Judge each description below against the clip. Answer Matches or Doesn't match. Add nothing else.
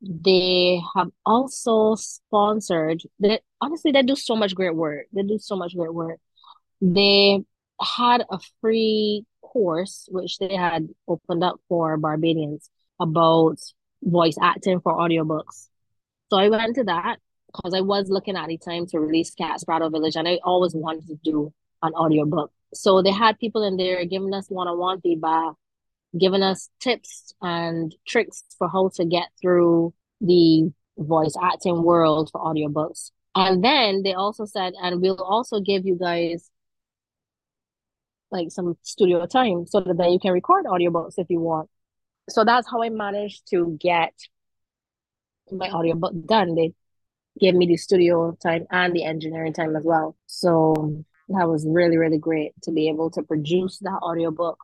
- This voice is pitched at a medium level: Matches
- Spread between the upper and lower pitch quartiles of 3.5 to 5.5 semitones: Doesn't match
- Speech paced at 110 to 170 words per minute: Matches